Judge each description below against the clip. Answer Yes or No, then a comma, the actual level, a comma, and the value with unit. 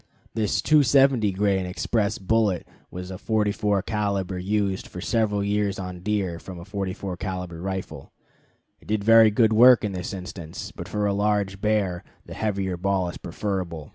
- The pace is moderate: Yes, average, 165 wpm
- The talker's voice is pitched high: No, low, 100 Hz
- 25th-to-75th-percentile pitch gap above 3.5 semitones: No, narrow, 2.5 semitones